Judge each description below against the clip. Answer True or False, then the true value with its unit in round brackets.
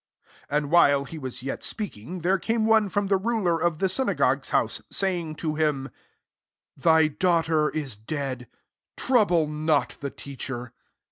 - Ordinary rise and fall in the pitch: True (4.9 semitones)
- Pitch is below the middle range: False (160 Hz)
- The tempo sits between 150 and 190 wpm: True (155 wpm)